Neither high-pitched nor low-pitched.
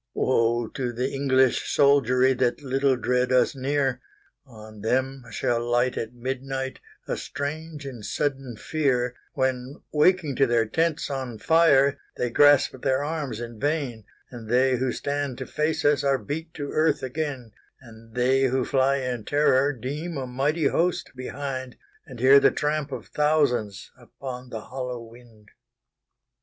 No: low, 130 Hz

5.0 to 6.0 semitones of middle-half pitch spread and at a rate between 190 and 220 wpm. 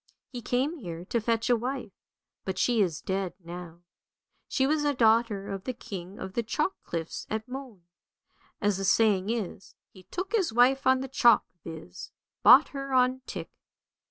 No: wide, 5.5 semitones; average, 180 wpm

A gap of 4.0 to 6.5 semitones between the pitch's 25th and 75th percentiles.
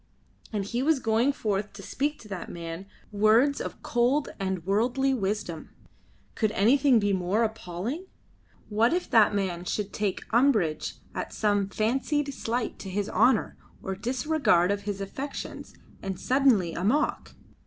Yes: average, 4.8 semitones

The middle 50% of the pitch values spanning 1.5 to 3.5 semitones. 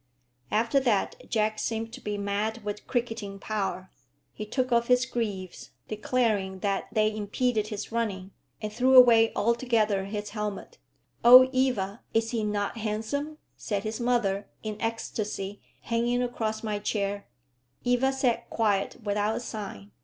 Yes: narrow, 2.6 semitones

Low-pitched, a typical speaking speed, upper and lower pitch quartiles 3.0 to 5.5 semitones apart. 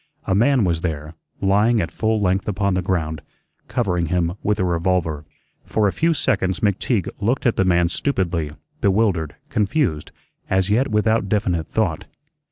Yes: very low, 95 Hz; average, 160 wpm; average, 4.0 semitones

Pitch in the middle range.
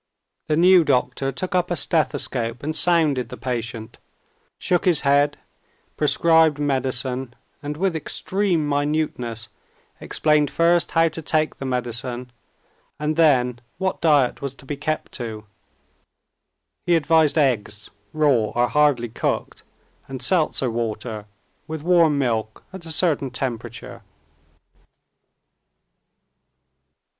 Yes: medium, 145 Hz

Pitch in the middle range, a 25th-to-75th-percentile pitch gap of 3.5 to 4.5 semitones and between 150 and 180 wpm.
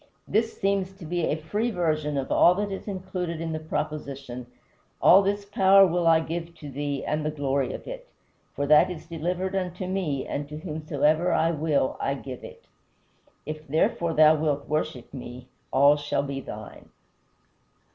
Yes: medium, 155 Hz; average, 4.0 semitones; average, 170 wpm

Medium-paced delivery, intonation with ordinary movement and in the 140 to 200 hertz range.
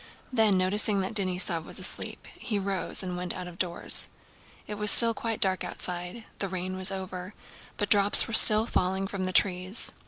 No: average, 185 wpm; narrow, 2.1 semitones; high, 190 Hz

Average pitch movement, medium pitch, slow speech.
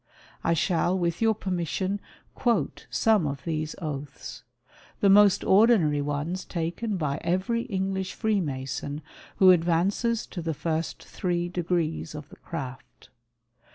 Yes: average, 3.9 semitones; medium, 175 Hz; slow, 130 wpm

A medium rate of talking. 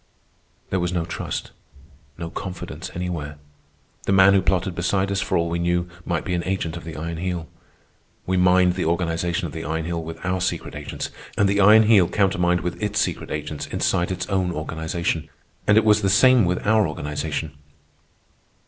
Yes: average, 185 wpm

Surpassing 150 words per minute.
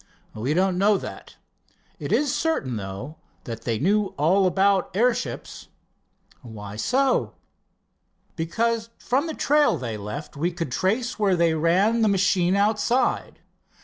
No: slow, 135 wpm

